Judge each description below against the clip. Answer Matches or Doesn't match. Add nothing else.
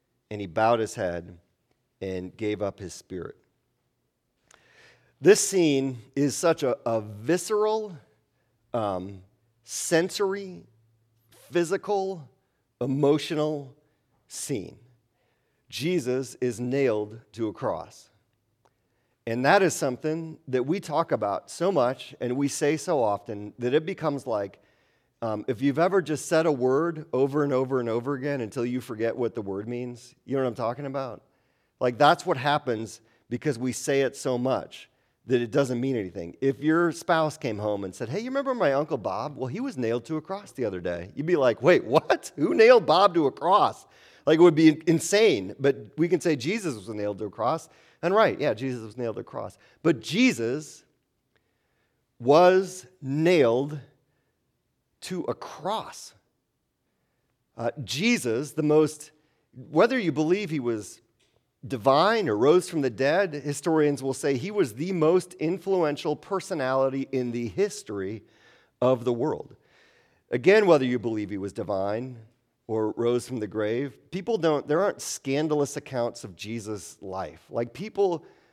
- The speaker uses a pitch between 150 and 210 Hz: Doesn't match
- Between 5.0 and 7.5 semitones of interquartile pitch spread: Matches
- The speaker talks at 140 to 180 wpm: Matches